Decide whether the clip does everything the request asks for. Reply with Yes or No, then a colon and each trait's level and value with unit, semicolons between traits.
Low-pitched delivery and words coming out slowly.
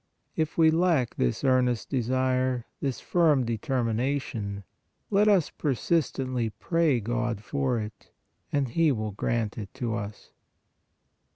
Yes: low, 125 Hz; slow, 120 wpm